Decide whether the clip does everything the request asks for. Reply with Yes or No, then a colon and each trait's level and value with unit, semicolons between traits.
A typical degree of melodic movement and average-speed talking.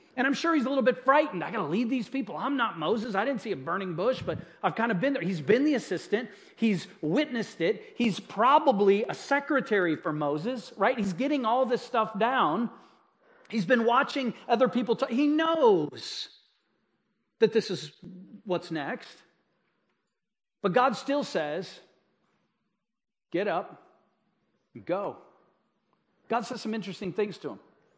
Yes: average, 5.0 semitones; average, 165 wpm